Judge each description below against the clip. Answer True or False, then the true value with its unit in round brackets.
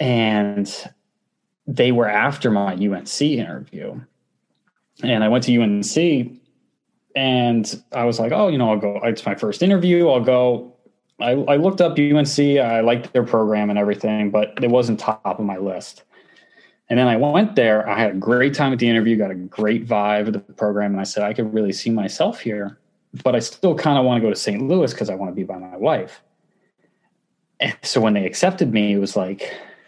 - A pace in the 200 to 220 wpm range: True (205 wpm)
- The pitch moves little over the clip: False (3.5 semitones)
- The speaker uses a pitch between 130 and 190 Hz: False (115 Hz)